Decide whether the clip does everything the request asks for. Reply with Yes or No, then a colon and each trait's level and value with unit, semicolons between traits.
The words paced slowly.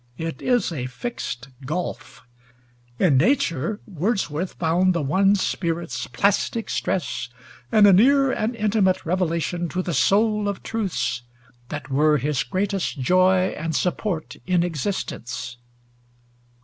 Yes: slow, 125 wpm